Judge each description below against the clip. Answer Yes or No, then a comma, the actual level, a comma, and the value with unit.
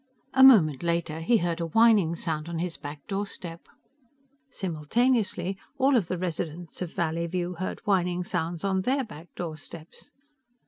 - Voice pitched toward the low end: No, medium, 175 Hz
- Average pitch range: Yes, average, 3.2 semitones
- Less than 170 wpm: Yes, average, 145 wpm